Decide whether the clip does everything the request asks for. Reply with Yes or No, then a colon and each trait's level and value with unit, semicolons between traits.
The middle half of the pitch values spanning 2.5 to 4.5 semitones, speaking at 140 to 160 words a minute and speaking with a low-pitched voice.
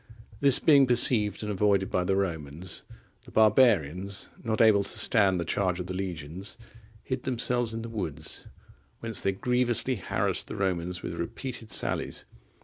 Yes: average, 4.1 semitones; average, 155 wpm; low, 100 Hz